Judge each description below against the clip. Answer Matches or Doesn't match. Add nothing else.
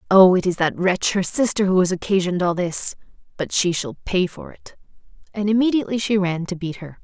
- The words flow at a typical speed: Doesn't match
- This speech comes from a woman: Matches